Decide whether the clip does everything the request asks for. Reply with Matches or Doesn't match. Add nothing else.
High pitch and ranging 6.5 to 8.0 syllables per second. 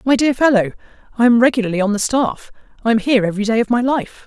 Matches